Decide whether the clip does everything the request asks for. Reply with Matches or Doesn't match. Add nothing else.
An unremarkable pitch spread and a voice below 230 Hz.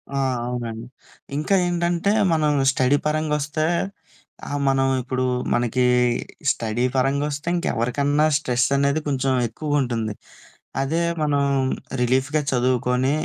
Matches